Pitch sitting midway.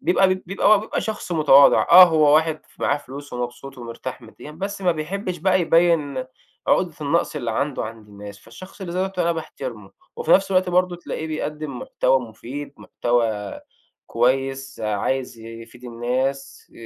Yes: medium, 145 Hz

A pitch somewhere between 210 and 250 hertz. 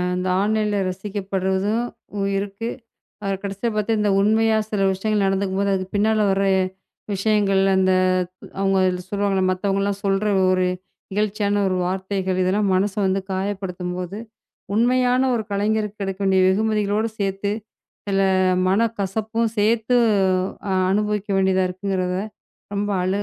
No: high, 200 Hz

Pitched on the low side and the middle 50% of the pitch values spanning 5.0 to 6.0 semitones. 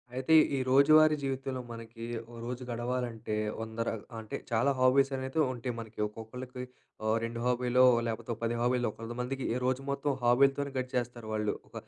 No: low, 125 Hz; narrow, 2.4 semitones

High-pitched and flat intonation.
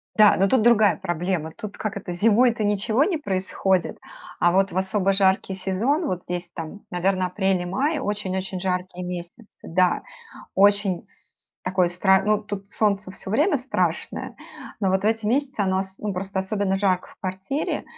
Yes: high, 195 Hz; narrow, 2.3 semitones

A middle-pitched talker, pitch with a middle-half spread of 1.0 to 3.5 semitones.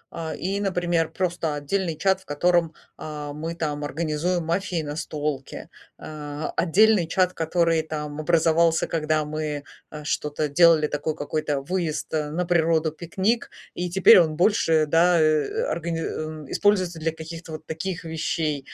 Yes: medium, 160 Hz; narrow, 2.4 semitones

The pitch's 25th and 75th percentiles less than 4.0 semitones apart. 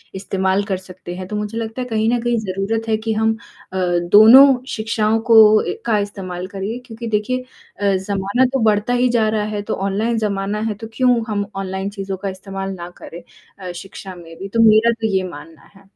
Yes: average, 2.7 semitones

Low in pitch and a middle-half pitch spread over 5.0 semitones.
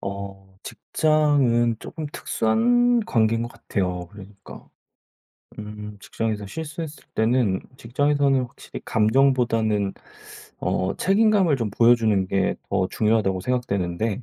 Yes: low, 115 Hz; wide, 5.6 semitones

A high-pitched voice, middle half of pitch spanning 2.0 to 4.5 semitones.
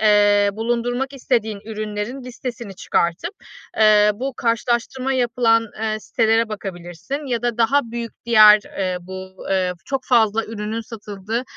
Yes: high, 225 Hz; narrow, 2.5 semitones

